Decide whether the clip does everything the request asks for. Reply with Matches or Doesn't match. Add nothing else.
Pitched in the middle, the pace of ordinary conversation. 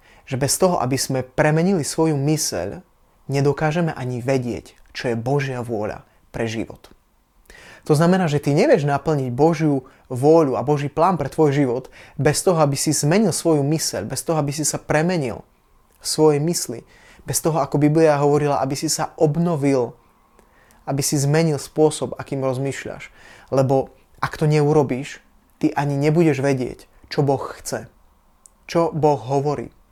Matches